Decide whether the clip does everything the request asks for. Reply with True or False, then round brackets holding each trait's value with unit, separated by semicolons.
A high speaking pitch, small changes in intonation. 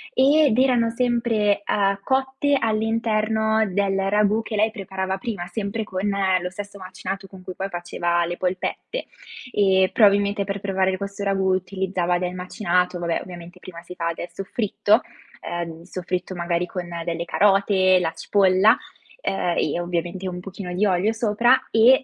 False (195 Hz; 3.0 semitones)